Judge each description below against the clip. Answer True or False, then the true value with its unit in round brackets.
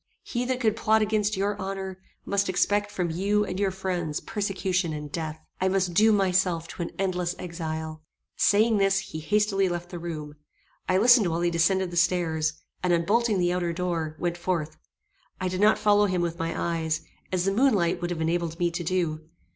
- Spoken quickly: False (195 wpm)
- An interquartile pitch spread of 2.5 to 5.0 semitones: True (3.0 semitones)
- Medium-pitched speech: True (180 Hz)